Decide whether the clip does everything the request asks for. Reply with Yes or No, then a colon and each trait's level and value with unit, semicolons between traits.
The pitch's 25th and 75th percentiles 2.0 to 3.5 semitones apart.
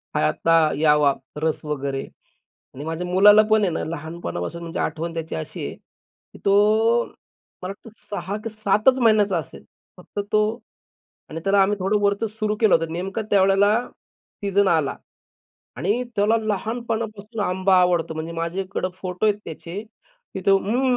No: average, 4.2 semitones